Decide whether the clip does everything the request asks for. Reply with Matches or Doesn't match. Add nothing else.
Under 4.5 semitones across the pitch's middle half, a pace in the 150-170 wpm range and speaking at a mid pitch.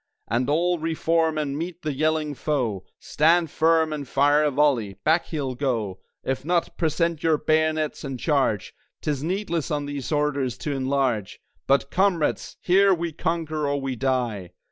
Matches